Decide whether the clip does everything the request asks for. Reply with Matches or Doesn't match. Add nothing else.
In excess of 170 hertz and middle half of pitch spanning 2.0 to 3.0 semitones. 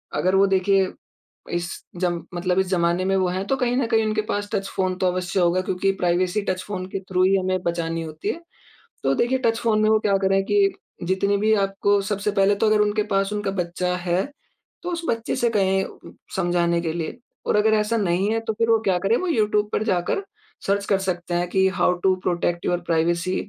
Matches